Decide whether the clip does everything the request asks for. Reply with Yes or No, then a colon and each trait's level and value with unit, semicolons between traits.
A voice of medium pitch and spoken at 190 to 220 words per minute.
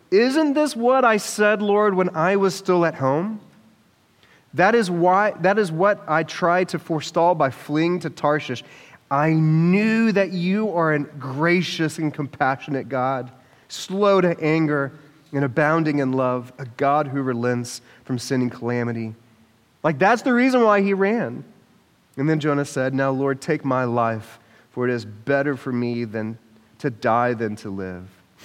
No: medium, 150 Hz; average, 170 wpm